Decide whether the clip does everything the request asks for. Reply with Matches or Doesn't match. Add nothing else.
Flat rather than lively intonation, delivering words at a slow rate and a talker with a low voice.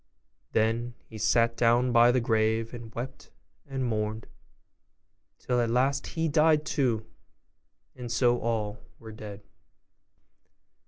Matches